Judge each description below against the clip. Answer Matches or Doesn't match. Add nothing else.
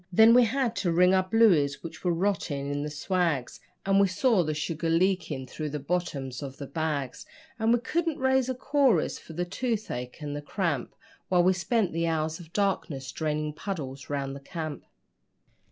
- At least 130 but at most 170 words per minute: Doesn't match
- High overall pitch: Doesn't match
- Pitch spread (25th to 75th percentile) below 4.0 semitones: Doesn't match